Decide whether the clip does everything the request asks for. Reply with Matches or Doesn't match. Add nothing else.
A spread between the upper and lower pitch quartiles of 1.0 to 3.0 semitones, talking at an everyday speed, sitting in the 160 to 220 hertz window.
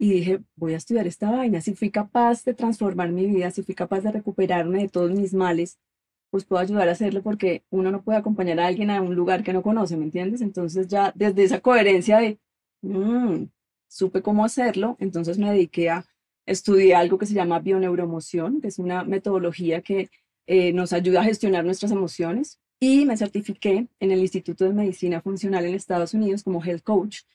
Doesn't match